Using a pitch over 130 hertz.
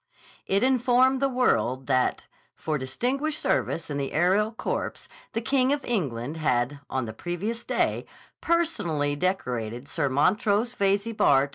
Yes: medium, 185 Hz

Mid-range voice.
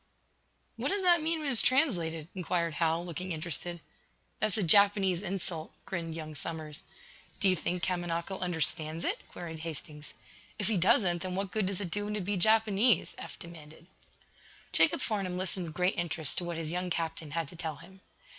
Yes: medium, 175 Hz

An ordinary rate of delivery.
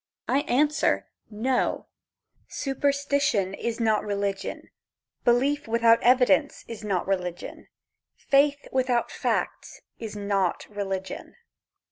No: slow, 95 wpm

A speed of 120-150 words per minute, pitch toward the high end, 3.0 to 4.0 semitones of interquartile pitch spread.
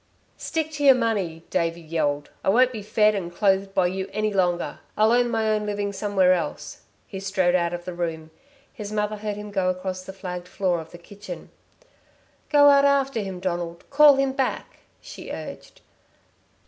No: average, 185 wpm; high, 195 Hz; average, 3.6 semitones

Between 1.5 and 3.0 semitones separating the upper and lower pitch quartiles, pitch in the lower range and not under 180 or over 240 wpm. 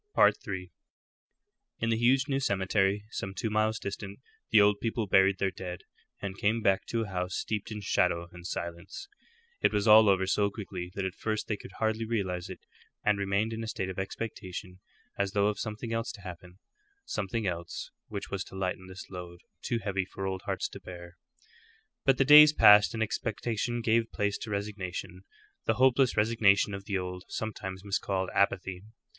Yes: average, 2.7 semitones; low, 100 Hz; average, 185 wpm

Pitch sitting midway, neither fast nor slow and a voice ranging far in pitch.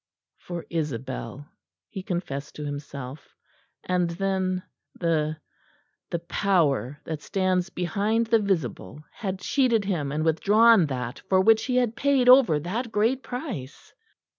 No: medium, 180 Hz; slow, 130 wpm; wide, 6.3 semitones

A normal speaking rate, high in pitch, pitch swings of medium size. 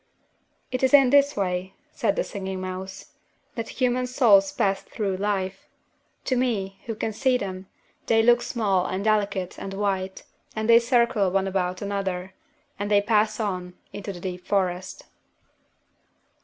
Yes: average, 155 wpm; high, 200 Hz; average, 3.3 semitones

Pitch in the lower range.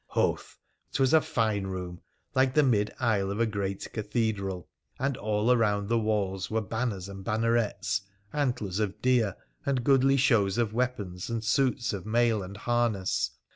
Yes: low, 110 Hz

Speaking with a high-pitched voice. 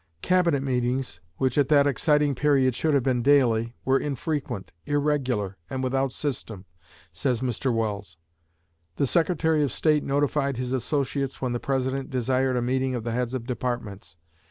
No: low, 130 Hz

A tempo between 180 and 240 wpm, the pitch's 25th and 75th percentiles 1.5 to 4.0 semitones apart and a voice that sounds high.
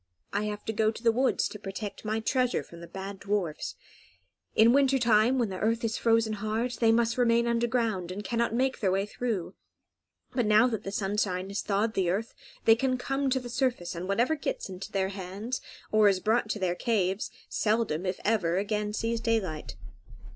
Yes: average, 195 wpm; average, 3.2 semitones; high, 215 Hz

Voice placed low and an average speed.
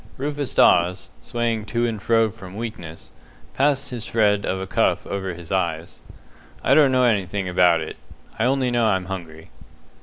Yes: low, 105 Hz; average, 170 wpm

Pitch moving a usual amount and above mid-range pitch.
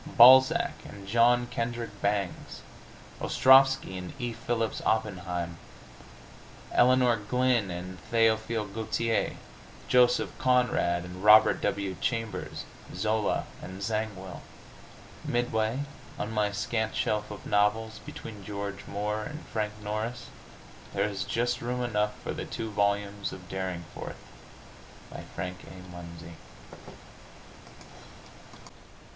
No: average, 3.2 semitones; low, 105 Hz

